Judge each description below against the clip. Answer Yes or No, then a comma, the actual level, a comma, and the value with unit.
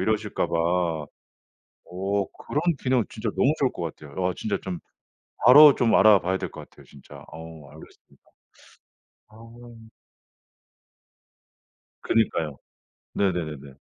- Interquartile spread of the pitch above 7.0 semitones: No, wide, 5.5 semitones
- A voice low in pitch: Yes, very low, 95 Hz